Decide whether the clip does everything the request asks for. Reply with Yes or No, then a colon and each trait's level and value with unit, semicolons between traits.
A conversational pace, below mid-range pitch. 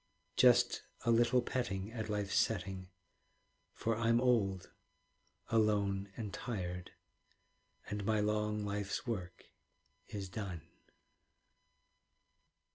No: slow, 95 wpm; low, 105 Hz